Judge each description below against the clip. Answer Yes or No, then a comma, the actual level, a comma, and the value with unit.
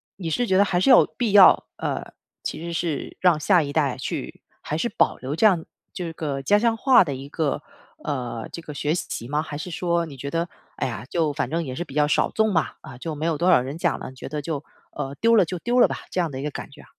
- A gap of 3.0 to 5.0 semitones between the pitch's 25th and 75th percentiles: Yes, average, 4.1 semitones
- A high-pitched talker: No, medium, 160 Hz